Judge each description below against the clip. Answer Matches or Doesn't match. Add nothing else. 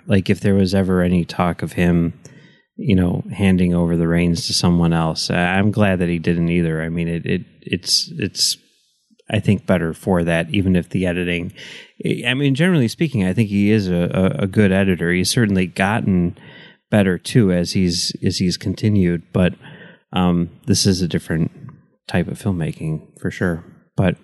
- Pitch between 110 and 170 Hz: Doesn't match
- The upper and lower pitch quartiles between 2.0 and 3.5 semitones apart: Matches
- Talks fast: Doesn't match